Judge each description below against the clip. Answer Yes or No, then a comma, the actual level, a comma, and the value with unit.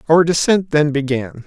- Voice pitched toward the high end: No, medium, 150 Hz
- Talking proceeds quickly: No, average, 165 wpm